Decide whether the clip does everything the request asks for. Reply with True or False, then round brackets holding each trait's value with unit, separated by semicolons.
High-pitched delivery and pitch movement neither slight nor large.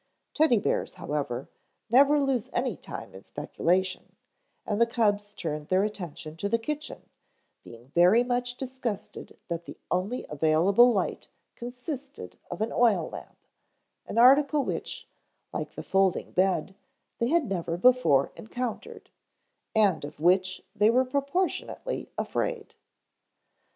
False (215 Hz; 5.9 semitones)